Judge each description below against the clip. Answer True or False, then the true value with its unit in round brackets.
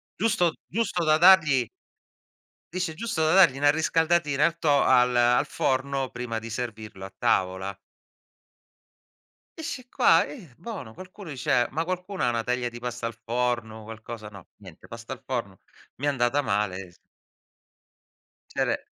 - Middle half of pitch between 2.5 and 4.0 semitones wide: False (6.3 semitones)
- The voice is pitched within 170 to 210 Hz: False (130 Hz)